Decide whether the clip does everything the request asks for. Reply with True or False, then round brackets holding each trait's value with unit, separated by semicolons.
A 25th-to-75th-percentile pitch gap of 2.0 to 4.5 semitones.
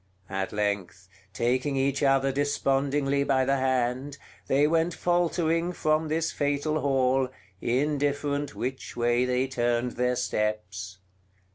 True (2.9 semitones)